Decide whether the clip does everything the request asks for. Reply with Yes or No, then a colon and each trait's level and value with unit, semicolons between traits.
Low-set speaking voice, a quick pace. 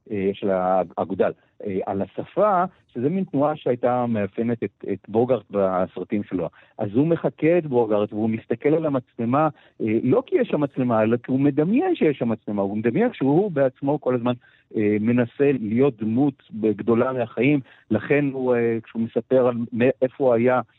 Yes: low, 120 Hz; fast, 160 wpm